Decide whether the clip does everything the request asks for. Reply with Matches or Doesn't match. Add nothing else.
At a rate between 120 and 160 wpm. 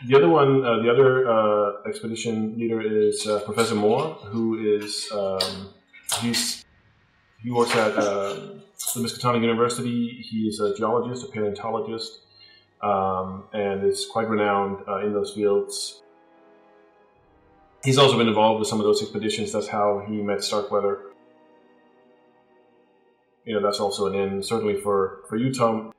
Matches